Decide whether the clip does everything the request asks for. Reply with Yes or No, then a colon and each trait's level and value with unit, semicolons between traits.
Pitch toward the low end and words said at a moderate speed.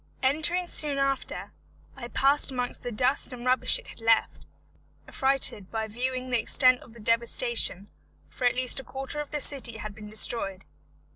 No: very high, 250 Hz; average, 170 wpm